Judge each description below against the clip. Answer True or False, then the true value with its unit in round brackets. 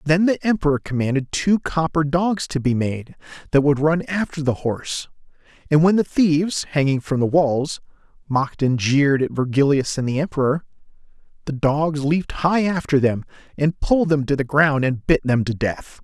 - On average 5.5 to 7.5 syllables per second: False (5.0 syllables/s)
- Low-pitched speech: False (145 Hz)